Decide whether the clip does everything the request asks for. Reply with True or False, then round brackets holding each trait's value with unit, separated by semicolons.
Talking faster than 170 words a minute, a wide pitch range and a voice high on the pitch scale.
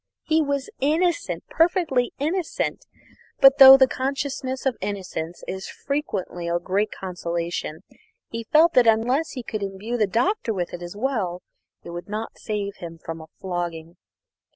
False (155 wpm; 7.5 semitones; 220 Hz)